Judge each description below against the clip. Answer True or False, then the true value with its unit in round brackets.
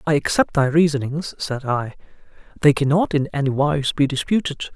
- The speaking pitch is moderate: True (145 Hz)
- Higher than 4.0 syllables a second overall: True (5.2 syllables/s)